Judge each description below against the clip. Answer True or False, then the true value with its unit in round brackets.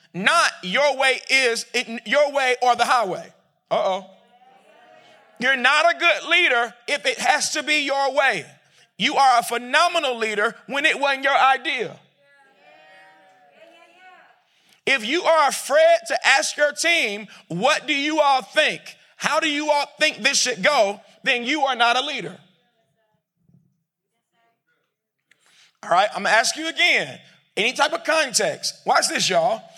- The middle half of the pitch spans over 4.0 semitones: True (5.0 semitones)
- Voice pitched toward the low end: False (270 Hz)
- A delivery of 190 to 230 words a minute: False (150 wpm)